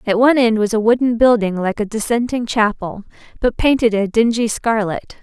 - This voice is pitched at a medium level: No, high, 225 Hz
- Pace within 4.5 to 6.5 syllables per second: Yes, 5.3 syllables/s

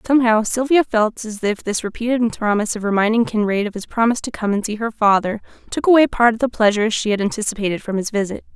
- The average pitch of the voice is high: Yes, high, 220 Hz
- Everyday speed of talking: No, fast, 225 wpm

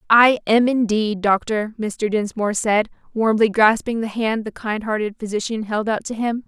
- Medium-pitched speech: No, high, 220 Hz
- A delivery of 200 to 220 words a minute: No, average, 175 wpm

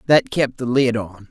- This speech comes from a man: Yes, male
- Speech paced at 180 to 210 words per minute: No, fast, 230 wpm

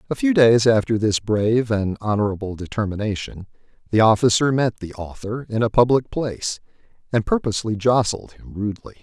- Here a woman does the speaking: No, male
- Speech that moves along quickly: No, average, 155 wpm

